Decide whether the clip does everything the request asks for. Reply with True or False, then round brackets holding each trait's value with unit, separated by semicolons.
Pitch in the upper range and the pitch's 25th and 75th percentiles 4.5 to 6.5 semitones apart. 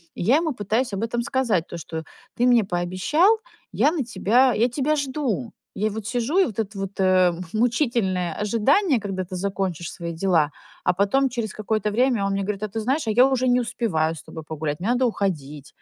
True (215 Hz; 5.0 semitones)